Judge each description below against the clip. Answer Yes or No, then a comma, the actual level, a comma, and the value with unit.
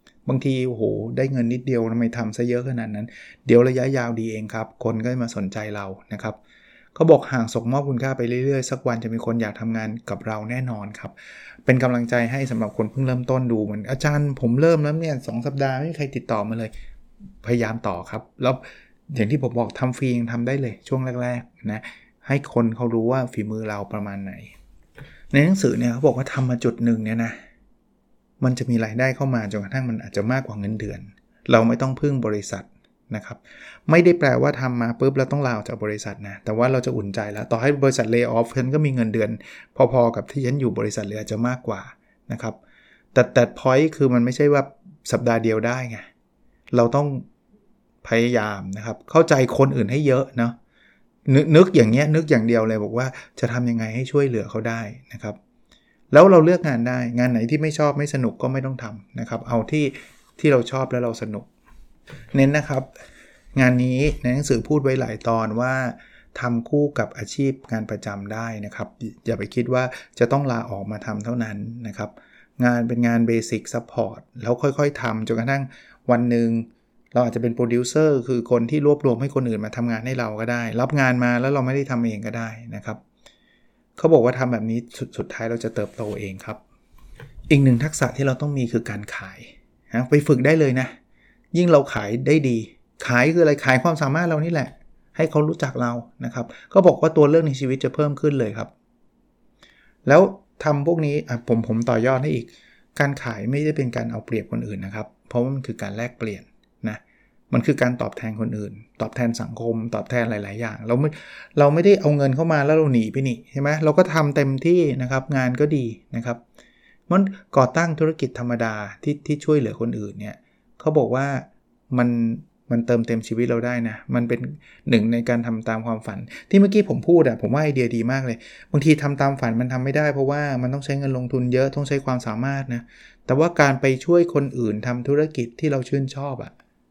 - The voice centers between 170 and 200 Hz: No, low, 125 Hz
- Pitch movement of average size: Yes, average, 3.3 semitones